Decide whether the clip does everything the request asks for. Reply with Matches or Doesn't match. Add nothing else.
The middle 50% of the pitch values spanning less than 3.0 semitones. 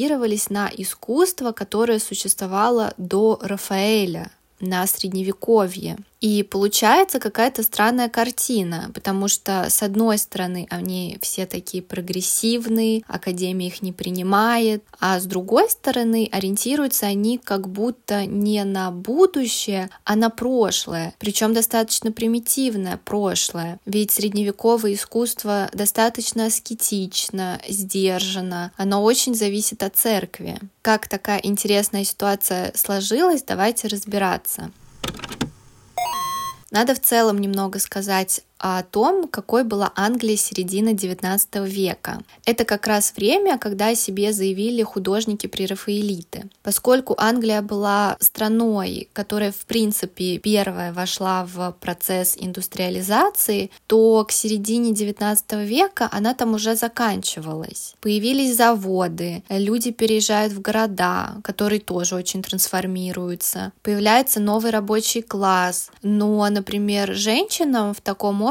Matches